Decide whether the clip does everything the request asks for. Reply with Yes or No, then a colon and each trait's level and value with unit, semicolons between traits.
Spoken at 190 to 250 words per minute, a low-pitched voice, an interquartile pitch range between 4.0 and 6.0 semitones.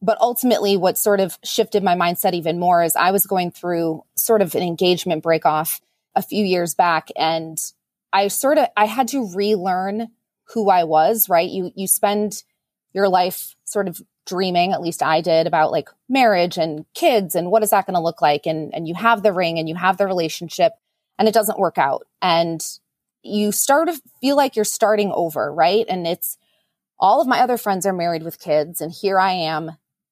No: fast, 205 wpm; high, 190 Hz; average, 4.3 semitones